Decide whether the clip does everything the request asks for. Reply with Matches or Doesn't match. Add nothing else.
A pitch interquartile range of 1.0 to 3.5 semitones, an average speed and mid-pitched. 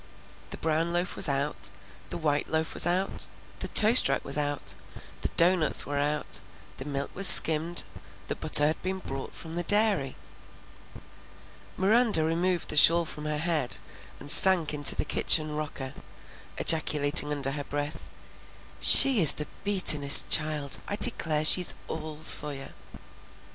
Matches